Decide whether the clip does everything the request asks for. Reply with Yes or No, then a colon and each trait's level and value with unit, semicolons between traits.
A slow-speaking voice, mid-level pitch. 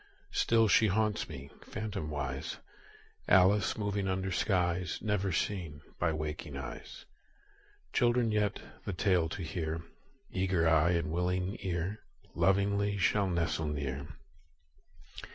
No: slow, 115 wpm; very low, 90 Hz